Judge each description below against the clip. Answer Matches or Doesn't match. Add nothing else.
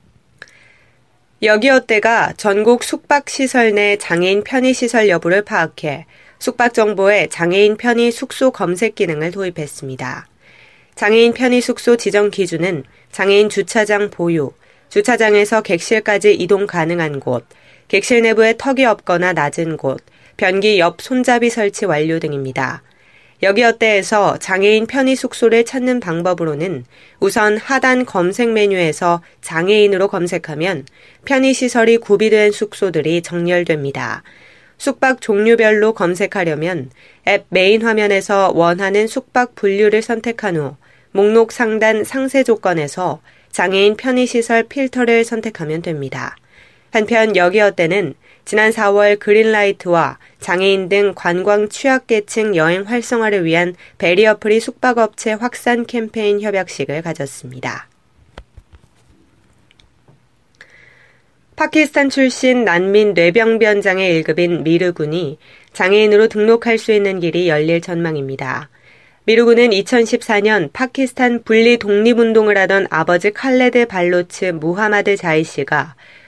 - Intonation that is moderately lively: Matches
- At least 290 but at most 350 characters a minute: Doesn't match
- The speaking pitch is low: Doesn't match